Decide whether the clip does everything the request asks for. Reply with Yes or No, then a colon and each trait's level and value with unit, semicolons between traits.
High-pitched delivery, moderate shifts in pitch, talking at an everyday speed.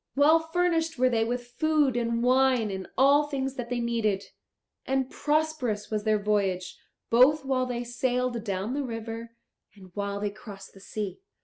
Yes: high, 240 Hz; average, 4.1 semitones; average, 170 wpm